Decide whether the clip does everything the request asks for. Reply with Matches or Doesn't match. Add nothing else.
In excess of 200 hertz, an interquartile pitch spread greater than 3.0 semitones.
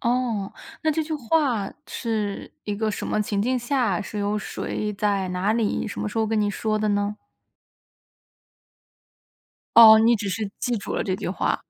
Doesn't match